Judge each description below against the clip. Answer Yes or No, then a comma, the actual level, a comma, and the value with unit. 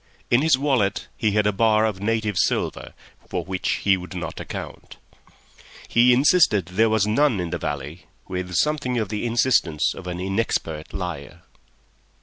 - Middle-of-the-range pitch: No, low, 105 Hz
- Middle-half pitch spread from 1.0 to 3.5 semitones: No, average, 4.5 semitones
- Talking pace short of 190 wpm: Yes, average, 160 wpm